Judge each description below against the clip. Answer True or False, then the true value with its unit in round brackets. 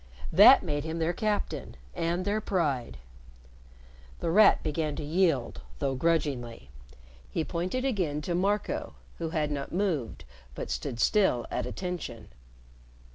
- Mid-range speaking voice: True (165 Hz)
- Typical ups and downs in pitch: True (4.2 semitones)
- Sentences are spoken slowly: True (130 wpm)